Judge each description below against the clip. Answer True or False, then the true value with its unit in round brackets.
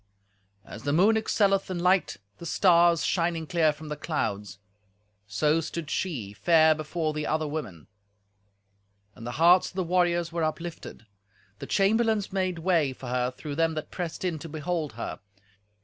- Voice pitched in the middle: True (165 Hz)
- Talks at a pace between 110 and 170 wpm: True (165 wpm)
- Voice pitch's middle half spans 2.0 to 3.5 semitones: True (3.0 semitones)